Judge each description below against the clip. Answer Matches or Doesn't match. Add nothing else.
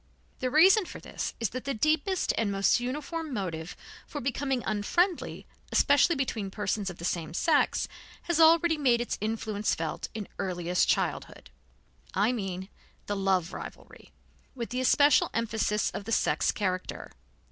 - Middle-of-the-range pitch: Doesn't match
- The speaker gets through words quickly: Doesn't match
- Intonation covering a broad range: Matches